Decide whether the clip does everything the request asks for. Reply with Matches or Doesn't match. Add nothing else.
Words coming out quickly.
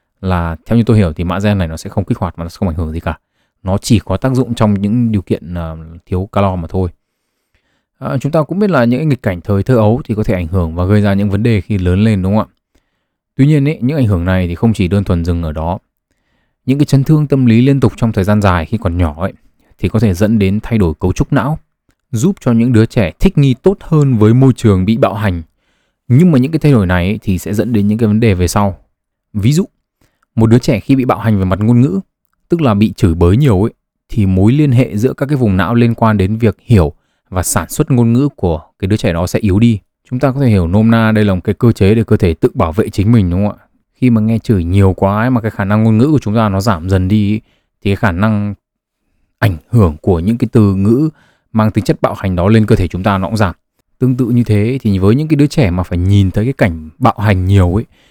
Matches